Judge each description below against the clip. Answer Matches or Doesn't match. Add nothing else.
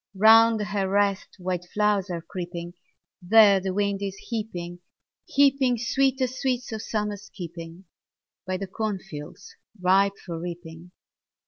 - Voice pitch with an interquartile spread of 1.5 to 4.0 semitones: Matches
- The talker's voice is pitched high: Matches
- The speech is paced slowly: Matches